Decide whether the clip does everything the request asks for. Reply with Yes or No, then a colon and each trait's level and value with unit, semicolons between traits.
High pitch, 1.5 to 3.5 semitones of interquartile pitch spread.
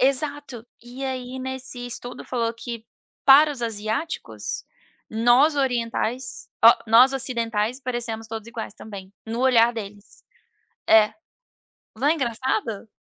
Yes: high, 240 Hz; average, 2.7 semitones